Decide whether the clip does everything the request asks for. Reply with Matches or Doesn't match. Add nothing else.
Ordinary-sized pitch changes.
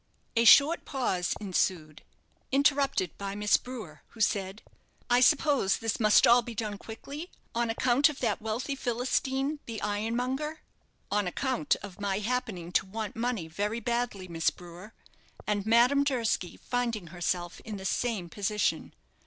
Matches